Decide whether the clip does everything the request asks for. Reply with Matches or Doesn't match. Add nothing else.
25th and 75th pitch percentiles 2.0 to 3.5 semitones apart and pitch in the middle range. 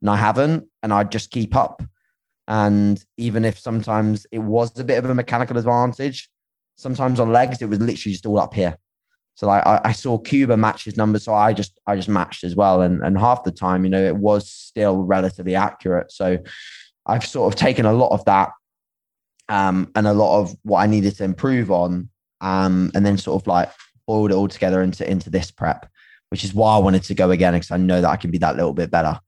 Doesn't match